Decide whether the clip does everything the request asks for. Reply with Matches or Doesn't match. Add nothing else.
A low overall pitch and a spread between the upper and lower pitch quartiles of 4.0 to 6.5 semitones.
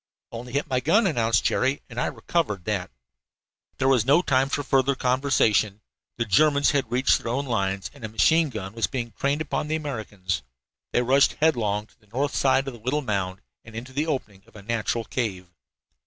Matches